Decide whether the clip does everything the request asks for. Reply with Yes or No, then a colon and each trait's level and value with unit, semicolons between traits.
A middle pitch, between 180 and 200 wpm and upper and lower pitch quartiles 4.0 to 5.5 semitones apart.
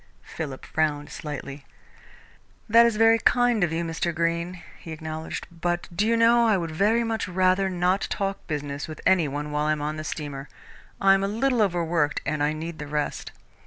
Yes: medium, 170 Hz; average, 195 wpm; average, 4.4 semitones